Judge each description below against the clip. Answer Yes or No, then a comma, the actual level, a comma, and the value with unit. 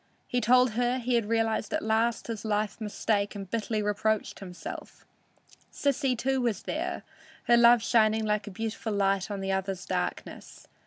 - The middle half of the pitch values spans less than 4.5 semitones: Yes, narrow, 2.4 semitones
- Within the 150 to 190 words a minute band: Yes, average, 160 wpm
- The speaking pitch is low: No, high, 220 Hz